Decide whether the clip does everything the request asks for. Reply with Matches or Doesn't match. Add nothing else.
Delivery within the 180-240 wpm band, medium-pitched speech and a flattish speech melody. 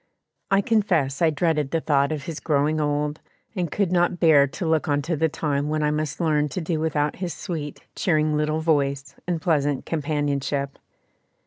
Matches